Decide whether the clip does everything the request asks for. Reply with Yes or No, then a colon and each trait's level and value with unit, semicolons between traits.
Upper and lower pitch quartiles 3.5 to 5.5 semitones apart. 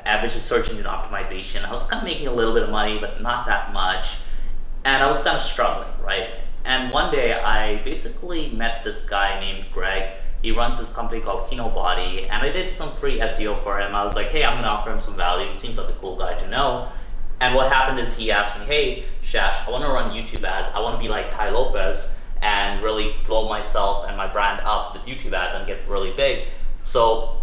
No: narrow, 2.6 semitones